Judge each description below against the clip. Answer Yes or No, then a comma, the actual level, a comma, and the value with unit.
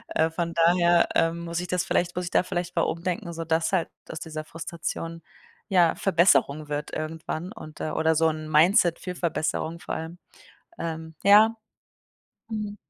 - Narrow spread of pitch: Yes, narrow, 1.7 semitones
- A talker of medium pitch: Yes, medium, 170 Hz